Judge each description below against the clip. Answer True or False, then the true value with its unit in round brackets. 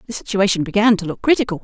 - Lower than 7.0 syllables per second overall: False (7.5 syllables/s)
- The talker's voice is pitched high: True (205 Hz)